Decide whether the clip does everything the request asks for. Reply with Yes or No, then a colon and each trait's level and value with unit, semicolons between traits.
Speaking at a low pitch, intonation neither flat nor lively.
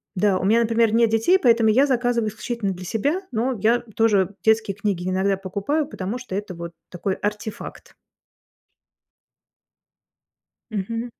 No: high, 220 Hz; average, 3.2 semitones